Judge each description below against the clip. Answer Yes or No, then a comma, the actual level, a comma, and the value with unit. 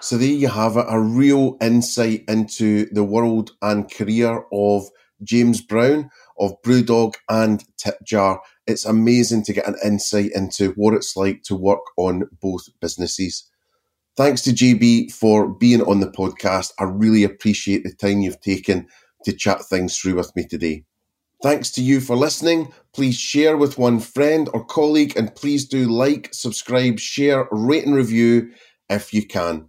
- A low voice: Yes, low, 110 Hz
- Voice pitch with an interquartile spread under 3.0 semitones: No, average, 3.6 semitones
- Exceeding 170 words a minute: No, average, 165 wpm